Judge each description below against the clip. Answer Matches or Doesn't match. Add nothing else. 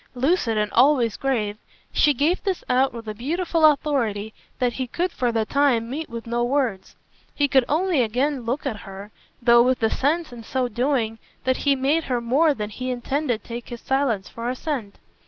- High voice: Matches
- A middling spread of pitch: Matches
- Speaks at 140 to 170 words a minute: Doesn't match